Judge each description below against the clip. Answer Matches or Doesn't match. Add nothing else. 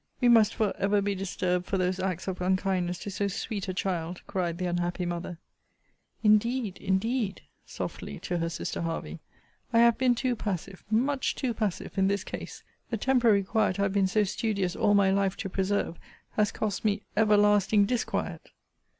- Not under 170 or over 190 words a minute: Matches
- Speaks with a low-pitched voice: Doesn't match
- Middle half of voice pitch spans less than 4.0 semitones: Matches